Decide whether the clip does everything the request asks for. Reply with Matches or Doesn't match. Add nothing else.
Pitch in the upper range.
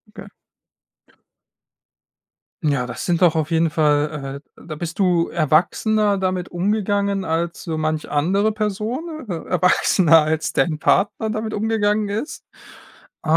Doesn't match